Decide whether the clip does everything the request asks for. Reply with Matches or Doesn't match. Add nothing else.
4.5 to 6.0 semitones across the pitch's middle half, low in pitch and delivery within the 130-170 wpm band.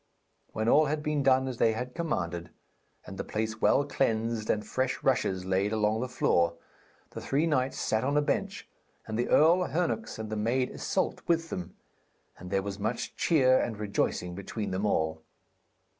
Doesn't match